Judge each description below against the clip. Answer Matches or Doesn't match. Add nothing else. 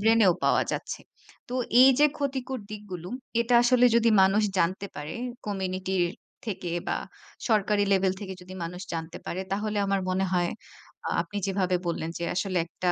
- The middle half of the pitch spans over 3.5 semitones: Doesn't match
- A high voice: Matches